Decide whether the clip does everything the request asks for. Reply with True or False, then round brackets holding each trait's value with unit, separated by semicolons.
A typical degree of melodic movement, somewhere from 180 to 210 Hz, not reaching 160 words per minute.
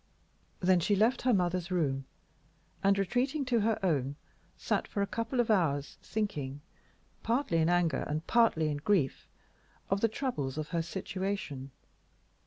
False (6.3 semitones; 185 Hz; 150 wpm)